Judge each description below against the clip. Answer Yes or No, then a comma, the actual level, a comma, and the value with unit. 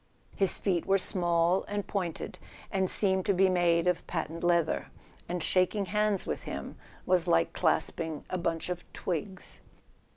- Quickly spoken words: No, average, 155 wpm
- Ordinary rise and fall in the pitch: No, narrow, 2.2 semitones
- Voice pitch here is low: No, medium, 180 Hz